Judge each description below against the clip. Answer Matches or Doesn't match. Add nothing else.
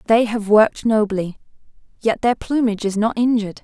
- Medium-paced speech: Matches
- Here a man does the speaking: Doesn't match